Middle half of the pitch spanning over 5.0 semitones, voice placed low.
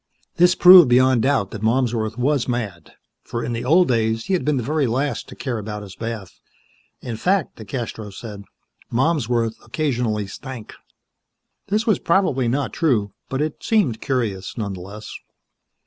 No: average, 4.7 semitones; low, 120 Hz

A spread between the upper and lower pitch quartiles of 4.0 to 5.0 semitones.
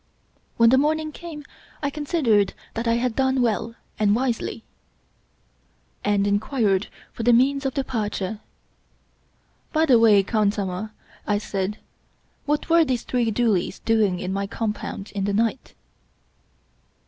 Yes: average, 4.4 semitones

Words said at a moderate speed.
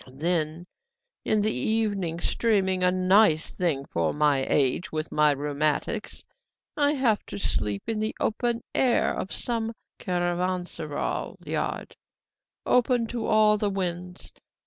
No: slow, 125 wpm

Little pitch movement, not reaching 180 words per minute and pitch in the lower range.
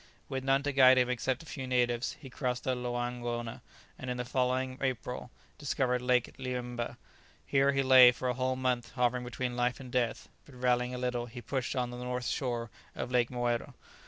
No: narrow, 1.1 semitones; average, 200 wpm; low, 125 Hz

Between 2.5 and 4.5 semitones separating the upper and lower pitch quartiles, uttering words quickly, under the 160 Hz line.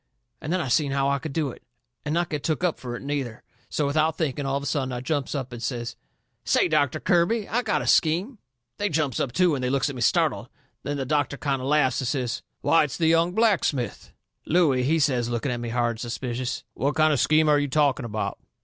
Yes: average, 3.7 semitones; fast, 250 wpm; medium, 140 Hz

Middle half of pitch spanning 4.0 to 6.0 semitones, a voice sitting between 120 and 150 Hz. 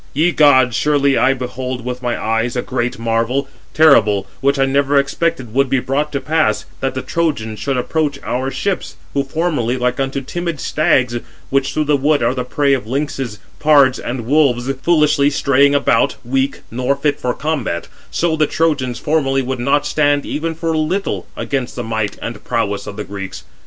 No: average, 3.2 semitones; low, 135 Hz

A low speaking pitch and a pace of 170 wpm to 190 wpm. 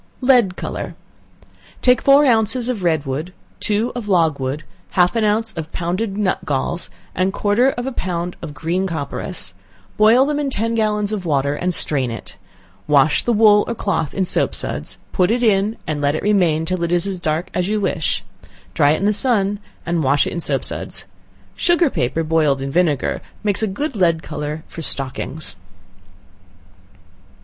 No: medium, 185 Hz; average, 180 wpm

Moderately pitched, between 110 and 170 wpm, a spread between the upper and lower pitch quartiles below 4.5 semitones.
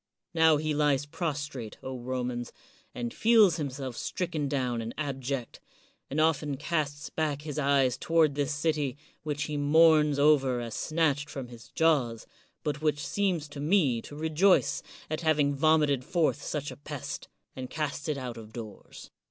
Yes: medium, 145 Hz; average, 160 wpm; average, 2.8 semitones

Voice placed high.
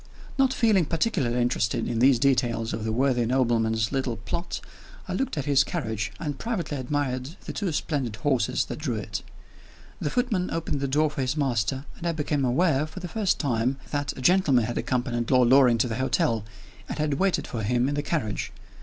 No: low, 135 Hz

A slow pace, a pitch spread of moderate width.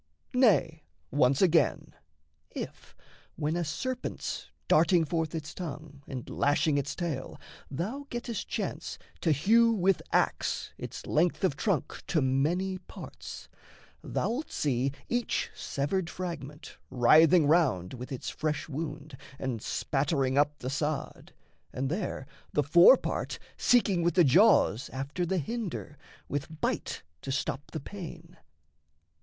Yes: slow, 130 wpm; average, 4.5 semitones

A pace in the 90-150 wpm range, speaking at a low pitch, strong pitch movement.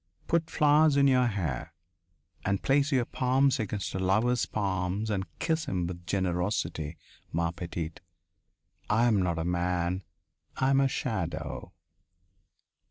Yes: slow, 135 wpm; low, 100 Hz; wide, 6.7 semitones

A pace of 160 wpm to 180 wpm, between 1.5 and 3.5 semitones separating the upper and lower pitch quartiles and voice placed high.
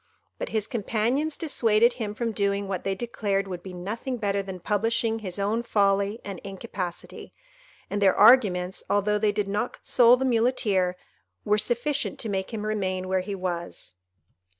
Yes: average, 165 wpm; average, 3.0 semitones; high, 205 Hz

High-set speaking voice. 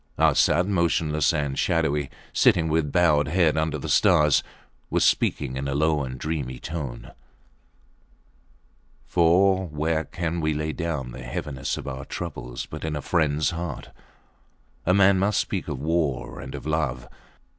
No: very low, 75 Hz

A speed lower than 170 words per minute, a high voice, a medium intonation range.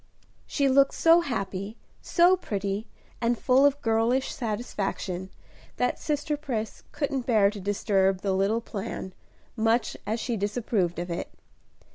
Yes: slow, 135 wpm; high, 225 Hz; average, 5.0 semitones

